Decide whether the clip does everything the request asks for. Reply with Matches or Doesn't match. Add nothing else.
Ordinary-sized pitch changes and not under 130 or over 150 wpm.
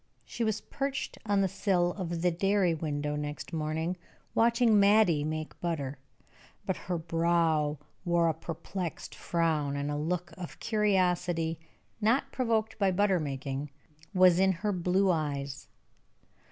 Matches